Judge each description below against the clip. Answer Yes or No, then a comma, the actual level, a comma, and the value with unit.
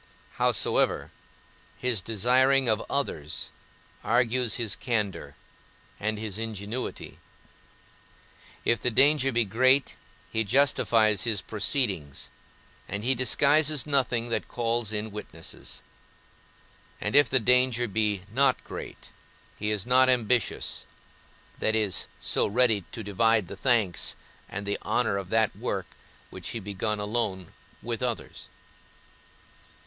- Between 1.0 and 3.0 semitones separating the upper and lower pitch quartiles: No, average, 3.4 semitones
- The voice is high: No, low, 115 Hz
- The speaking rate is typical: No, slow, 120 wpm